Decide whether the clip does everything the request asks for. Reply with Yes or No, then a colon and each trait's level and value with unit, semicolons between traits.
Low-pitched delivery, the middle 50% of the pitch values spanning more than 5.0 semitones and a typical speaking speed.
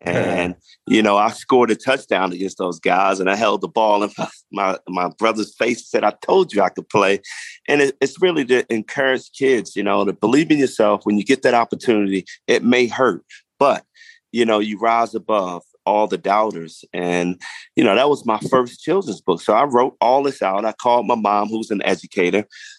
No: low, 115 Hz; wide, 5.4 semitones; fast, 210 wpm